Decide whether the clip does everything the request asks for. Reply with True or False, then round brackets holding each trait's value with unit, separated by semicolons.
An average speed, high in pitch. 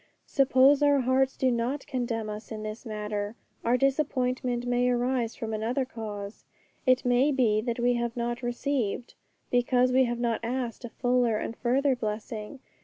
True (170 wpm; 245 Hz)